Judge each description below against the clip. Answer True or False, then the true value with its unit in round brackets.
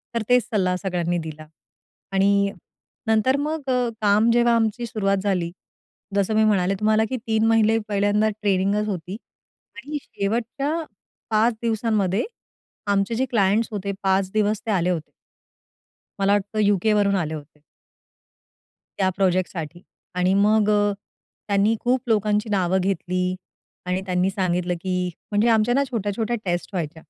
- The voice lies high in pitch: True (205 Hz)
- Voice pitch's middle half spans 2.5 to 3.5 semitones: True (3.0 semitones)